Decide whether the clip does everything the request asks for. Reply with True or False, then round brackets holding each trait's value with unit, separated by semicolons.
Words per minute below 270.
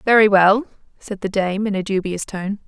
True (200 wpm)